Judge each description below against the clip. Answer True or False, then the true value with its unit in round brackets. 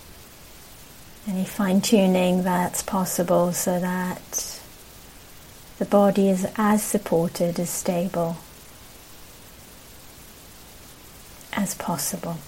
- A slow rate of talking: True (75 wpm)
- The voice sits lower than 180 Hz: False (185 Hz)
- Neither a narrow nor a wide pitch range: False (2.1 semitones)